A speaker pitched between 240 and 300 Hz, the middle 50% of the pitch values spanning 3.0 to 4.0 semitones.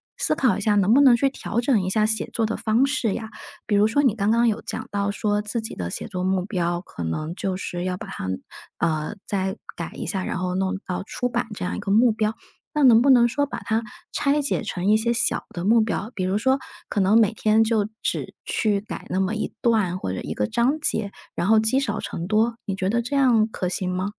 No: high, 215 Hz; average, 3.7 semitones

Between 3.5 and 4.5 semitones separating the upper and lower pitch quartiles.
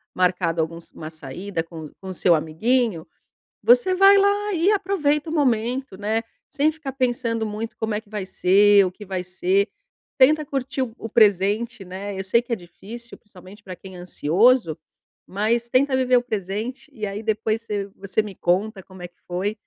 No: average, 5.2 semitones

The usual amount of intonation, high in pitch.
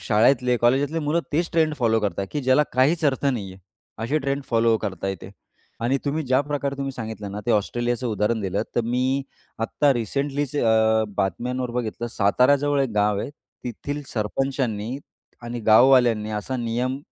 No: average, 3.8 semitones; low, 125 Hz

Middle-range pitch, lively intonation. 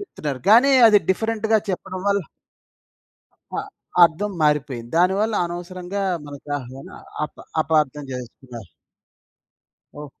Yes: medium, 170 Hz; wide, 5.9 semitones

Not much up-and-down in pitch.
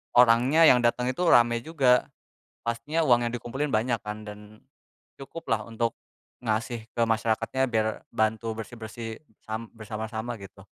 Yes: narrow, 2.1 semitones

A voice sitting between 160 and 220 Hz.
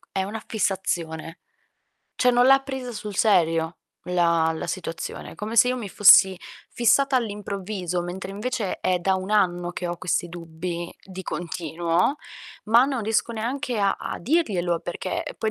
Yes: high, 190 Hz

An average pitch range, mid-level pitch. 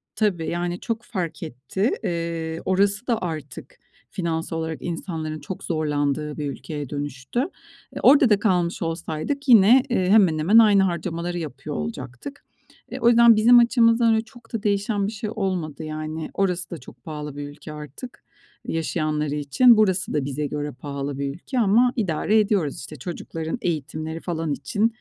No: wide, 5.8 semitones; medium, 170 Hz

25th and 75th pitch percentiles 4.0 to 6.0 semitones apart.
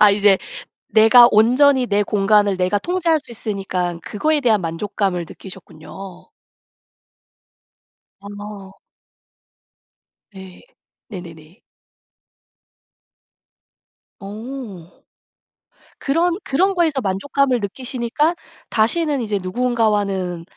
Yes: average, 5.1 semitones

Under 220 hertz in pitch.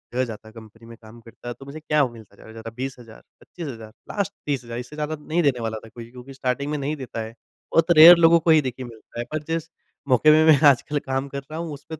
Yes: low, 135 Hz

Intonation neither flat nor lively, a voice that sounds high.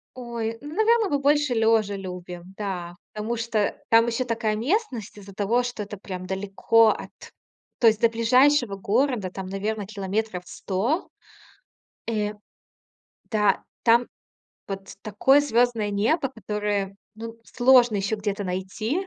Yes: average, 3.4 semitones; high, 220 Hz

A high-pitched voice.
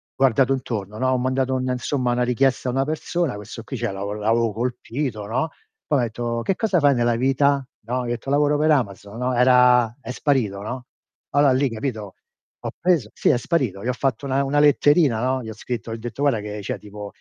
No: low, 125 Hz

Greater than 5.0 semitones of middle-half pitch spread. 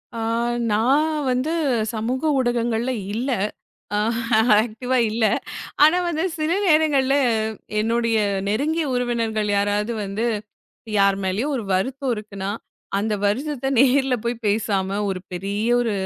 No: average, 4.2 semitones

